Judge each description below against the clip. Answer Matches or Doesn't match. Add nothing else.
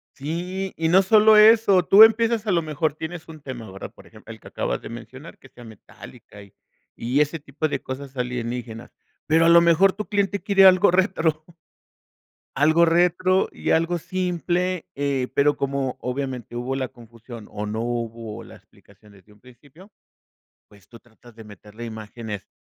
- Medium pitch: Matches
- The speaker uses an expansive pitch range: Matches